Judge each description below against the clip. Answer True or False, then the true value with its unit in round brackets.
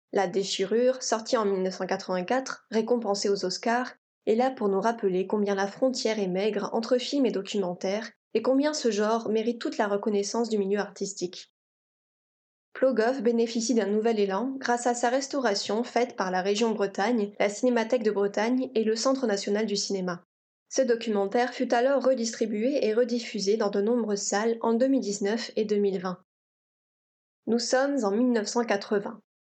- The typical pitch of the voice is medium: False (220 Hz)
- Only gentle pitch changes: False (3.3 semitones)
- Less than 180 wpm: True (155 wpm)